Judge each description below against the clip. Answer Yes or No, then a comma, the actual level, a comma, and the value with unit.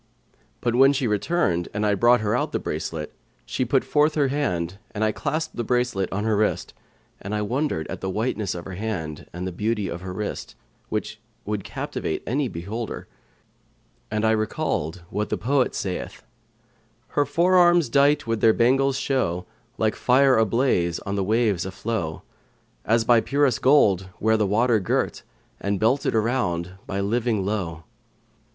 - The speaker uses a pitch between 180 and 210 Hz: No, low, 110 Hz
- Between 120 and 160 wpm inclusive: No, average, 175 wpm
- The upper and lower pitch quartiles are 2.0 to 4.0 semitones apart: No, average, 4.7 semitones